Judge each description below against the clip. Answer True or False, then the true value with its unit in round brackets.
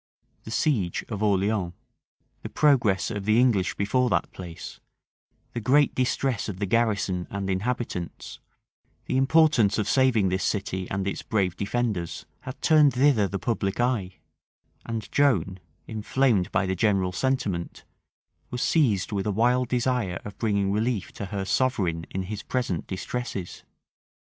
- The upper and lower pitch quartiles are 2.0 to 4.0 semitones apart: False (4.6 semitones)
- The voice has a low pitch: True (105 Hz)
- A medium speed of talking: True (145 wpm)